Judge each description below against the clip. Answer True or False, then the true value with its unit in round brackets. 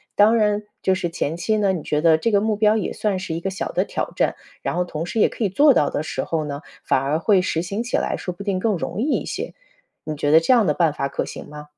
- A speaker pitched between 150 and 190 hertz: True (185 Hz)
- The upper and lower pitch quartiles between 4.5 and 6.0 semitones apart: True (4.9 semitones)